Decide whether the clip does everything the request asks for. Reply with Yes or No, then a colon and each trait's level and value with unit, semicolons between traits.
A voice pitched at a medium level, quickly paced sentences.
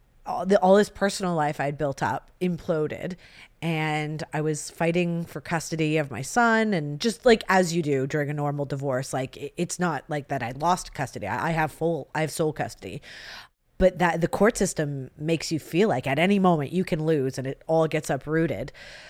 No: medium, 160 Hz; average, 195 wpm